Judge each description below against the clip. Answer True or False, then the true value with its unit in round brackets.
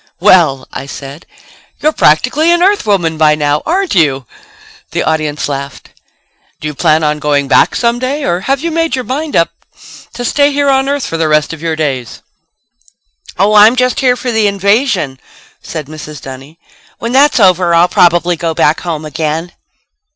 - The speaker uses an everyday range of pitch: False (8.8 semitones)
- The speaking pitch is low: False (175 Hz)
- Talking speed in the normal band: True (175 wpm)